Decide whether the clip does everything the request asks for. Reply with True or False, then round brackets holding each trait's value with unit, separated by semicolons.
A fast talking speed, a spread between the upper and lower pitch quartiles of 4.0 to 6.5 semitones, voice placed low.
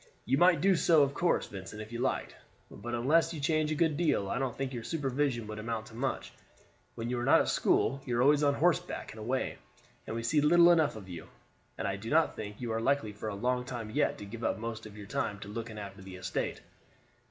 True (245 wpm; 5.2 semitones; 120 Hz)